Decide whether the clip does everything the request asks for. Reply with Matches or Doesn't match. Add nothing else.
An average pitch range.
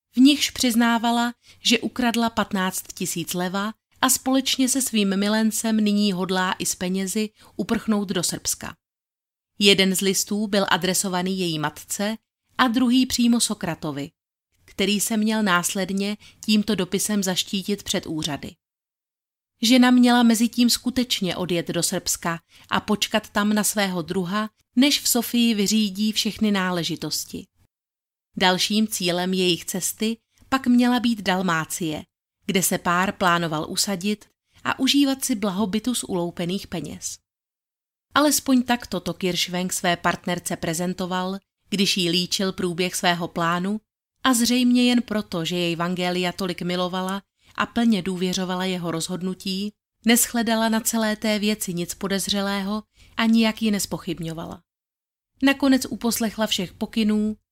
Matches